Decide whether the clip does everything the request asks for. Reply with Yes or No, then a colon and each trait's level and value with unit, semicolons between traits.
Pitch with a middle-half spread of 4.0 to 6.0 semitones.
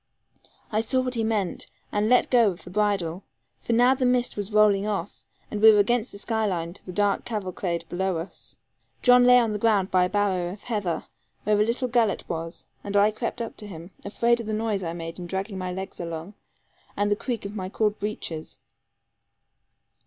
No: average, 3.3 semitones